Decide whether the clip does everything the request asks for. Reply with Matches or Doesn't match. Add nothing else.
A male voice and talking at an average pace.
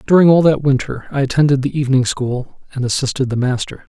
Matches